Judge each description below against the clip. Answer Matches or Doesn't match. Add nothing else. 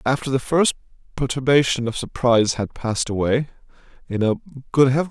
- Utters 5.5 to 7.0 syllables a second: Matches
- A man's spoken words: Matches